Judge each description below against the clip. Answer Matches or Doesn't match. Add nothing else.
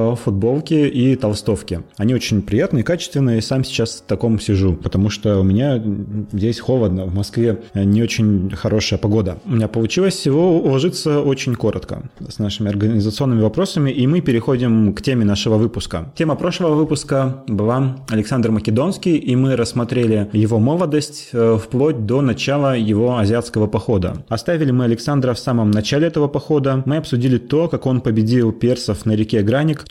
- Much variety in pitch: Doesn't match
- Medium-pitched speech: Doesn't match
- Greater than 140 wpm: Matches